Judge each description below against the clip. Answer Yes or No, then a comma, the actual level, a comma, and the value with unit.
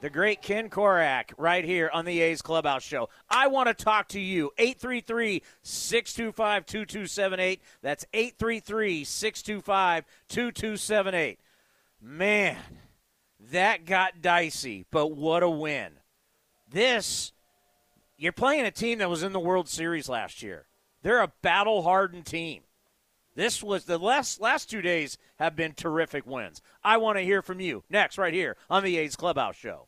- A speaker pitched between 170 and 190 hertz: Yes, medium, 185 Hz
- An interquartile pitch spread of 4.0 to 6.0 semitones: Yes, average, 4.4 semitones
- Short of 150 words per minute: Yes, average, 140 wpm